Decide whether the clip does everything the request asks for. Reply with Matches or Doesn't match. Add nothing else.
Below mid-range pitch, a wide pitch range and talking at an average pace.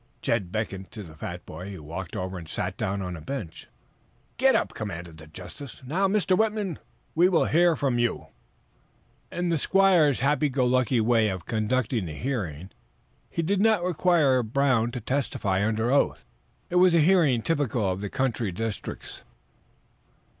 Matches